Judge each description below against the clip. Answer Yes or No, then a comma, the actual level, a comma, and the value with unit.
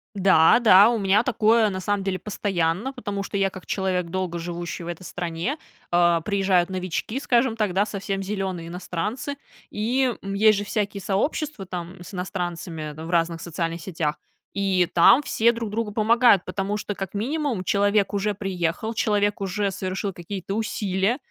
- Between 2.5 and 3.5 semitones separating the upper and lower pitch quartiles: Yes, average, 3.1 semitones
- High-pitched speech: Yes, high, 195 Hz